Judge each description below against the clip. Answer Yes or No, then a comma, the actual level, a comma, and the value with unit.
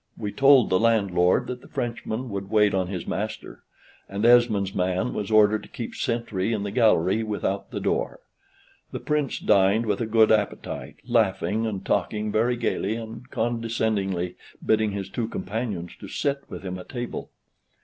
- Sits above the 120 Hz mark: No, low, 110 Hz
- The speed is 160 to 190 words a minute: Yes, average, 170 wpm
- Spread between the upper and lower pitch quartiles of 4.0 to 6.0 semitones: No, average, 2.9 semitones